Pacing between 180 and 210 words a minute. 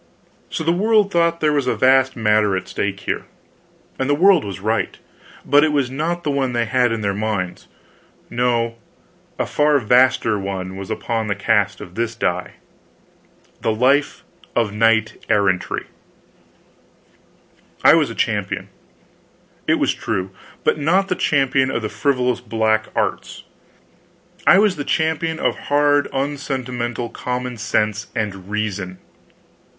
No: average, 145 wpm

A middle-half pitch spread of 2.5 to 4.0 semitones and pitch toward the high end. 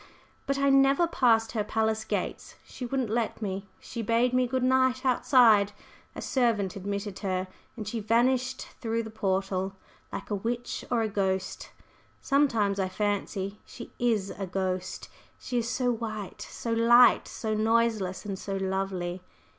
Yes: average, 3.7 semitones; high, 220 Hz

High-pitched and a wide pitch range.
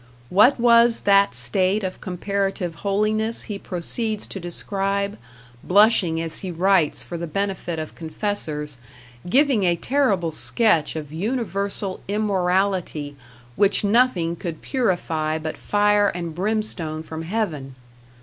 No: high, 195 Hz; average, 4.1 semitones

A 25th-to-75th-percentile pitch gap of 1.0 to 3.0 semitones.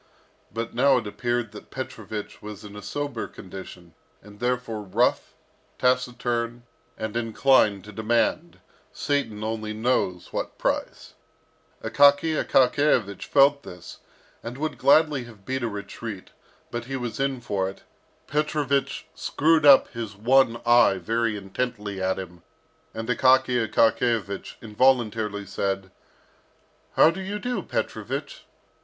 No: average, 4.1 semitones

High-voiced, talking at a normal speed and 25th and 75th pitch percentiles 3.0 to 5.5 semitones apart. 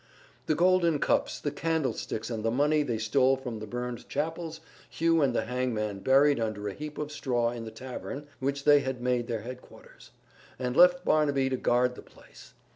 No: low, 130 Hz; average, 190 wpm; average, 3.8 semitones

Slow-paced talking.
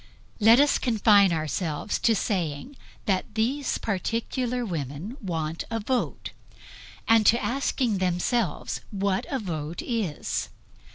Yes: slow, 115 wpm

